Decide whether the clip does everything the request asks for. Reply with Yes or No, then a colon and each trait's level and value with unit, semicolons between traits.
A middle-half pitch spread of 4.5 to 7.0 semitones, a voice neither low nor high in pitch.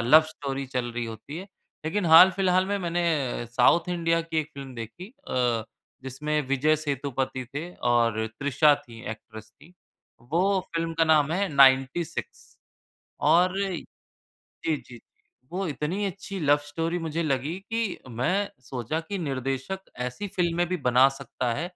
Yes: average, 5.0 semitones; medium, 150 Hz